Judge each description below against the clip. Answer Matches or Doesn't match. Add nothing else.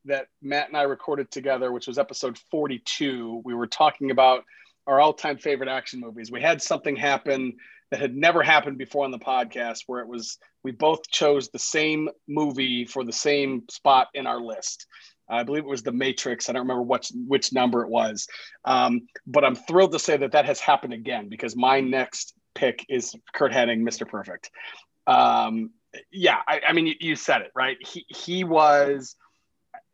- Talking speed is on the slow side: Doesn't match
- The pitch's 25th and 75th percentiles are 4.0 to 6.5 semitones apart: Doesn't match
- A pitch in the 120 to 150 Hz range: Matches